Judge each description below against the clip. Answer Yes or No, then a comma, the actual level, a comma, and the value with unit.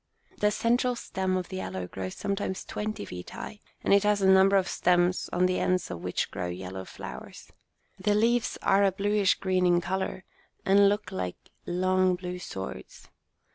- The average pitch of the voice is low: No, medium, 185 Hz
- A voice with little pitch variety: Yes, narrow, 2.3 semitones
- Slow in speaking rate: No, average, 175 wpm